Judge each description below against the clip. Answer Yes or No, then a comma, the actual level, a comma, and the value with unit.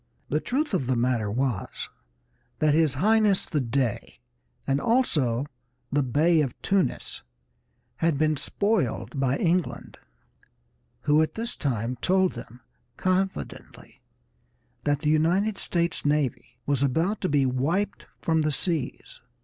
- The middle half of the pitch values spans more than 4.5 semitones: Yes, wide, 5.6 semitones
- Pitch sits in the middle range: Yes, medium, 150 Hz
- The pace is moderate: No, slow, 130 wpm